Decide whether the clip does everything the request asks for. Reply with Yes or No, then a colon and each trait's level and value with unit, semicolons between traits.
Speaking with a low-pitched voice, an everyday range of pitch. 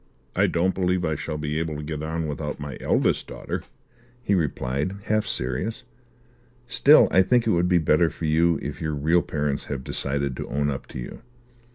Yes: very low, 80 Hz; average, 3.5 semitones